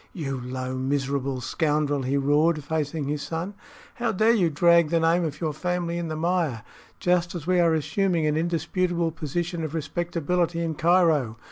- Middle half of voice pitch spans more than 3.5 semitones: No, average, 3.0 semitones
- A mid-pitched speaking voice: Yes, medium, 160 Hz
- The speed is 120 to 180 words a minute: Yes, average, 170 wpm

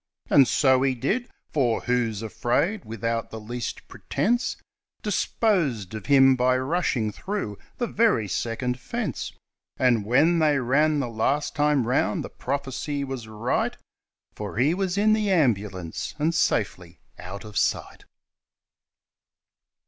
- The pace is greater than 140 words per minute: No, slow, 135 wpm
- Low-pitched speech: Yes, low, 130 Hz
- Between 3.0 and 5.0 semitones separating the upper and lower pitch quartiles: No, wide, 5.6 semitones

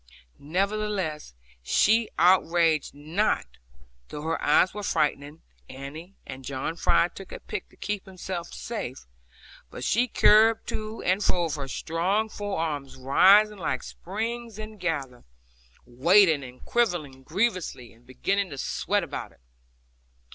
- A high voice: No, medium, 175 Hz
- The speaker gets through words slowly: Yes, slow, 130 wpm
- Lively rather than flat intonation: Yes, wide, 6.5 semitones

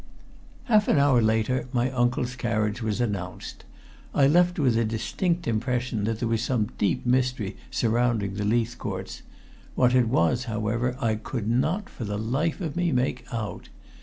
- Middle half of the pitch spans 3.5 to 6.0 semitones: No, average, 2.9 semitones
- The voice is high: No, low, 120 Hz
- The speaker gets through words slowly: No, average, 165 wpm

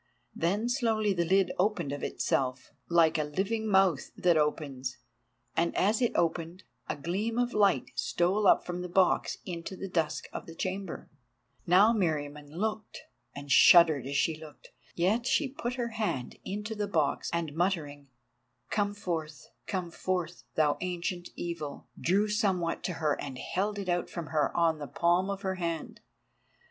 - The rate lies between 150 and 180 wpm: Yes, average, 160 wpm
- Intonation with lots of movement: No, average, 4.2 semitones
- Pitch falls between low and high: Yes, medium, 175 Hz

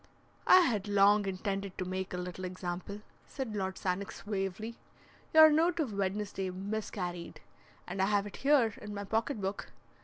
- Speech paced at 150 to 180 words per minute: Yes, average, 160 wpm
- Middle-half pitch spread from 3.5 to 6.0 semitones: No, narrow, 2.5 semitones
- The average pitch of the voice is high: Yes, high, 200 Hz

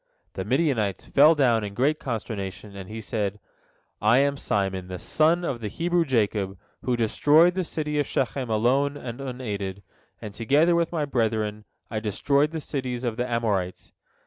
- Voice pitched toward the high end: No, low, 120 Hz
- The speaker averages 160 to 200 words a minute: Yes, average, 170 wpm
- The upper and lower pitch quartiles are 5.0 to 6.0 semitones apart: Yes, wide, 5.5 semitones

